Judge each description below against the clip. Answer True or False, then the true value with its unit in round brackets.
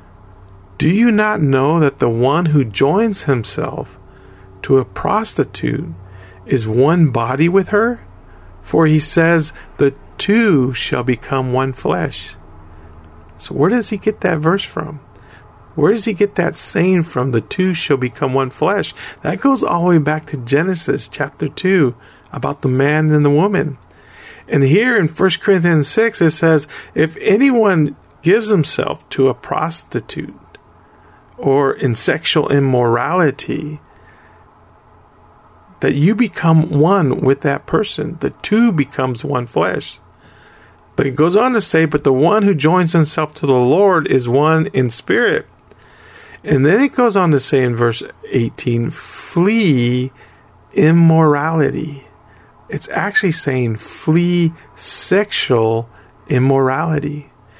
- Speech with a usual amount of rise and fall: False (5.7 semitones)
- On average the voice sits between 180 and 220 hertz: False (145 Hz)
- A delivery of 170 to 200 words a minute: False (140 wpm)